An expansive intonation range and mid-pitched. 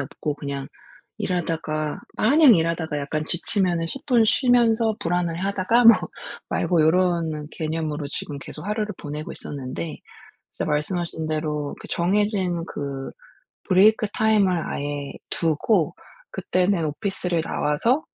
No: average, 5.0 semitones; medium, 170 Hz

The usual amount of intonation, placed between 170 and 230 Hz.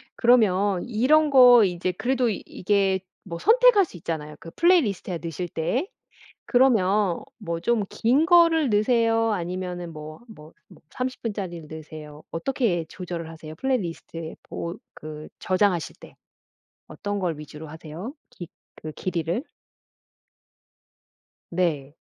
No: wide, 6.3 semitones; medium, 185 Hz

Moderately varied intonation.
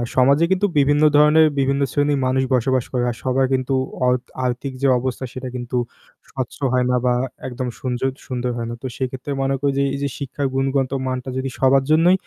No: narrow, 1.7 semitones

